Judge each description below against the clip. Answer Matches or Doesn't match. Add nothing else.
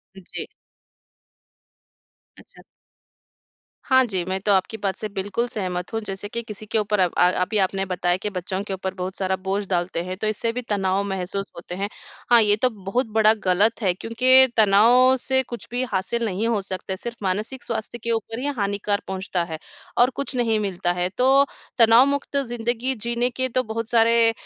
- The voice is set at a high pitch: Matches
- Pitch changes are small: Doesn't match